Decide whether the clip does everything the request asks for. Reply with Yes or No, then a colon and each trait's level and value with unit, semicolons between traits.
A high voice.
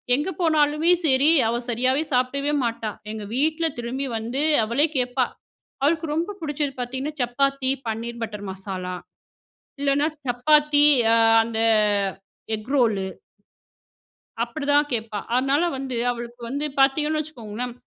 Yes: very high, 260 Hz